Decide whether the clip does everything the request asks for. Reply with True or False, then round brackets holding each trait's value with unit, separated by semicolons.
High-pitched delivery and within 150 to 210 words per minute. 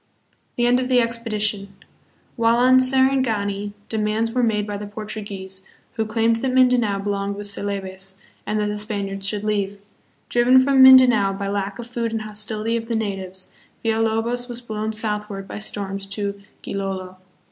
True (215 Hz; 165 wpm)